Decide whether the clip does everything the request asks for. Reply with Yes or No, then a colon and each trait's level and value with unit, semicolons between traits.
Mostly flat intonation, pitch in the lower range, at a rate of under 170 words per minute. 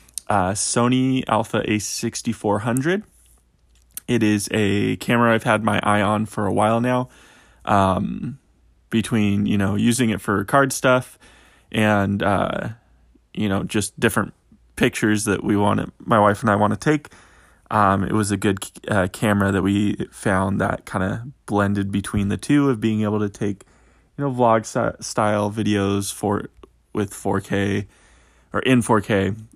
Yes: narrow, 2.3 semitones; low, 105 Hz; average, 155 wpm